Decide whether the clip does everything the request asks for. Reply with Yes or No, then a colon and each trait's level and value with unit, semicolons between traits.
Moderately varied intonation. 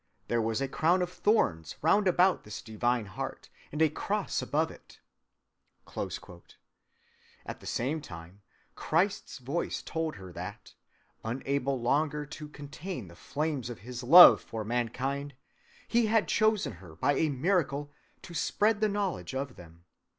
No: wide, 6.6 semitones